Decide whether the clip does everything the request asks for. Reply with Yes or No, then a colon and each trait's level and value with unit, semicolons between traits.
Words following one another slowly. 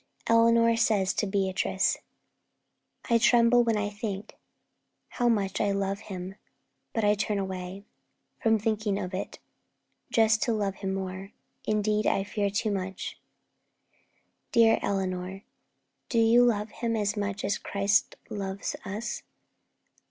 Yes: slow, 130 wpm